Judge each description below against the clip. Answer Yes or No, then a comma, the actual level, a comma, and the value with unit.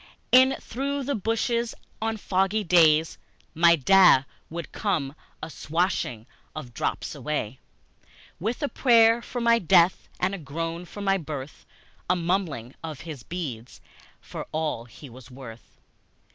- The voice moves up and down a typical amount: No, wide, 6.7 semitones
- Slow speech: No, average, 145 wpm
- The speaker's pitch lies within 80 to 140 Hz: No, medium, 170 Hz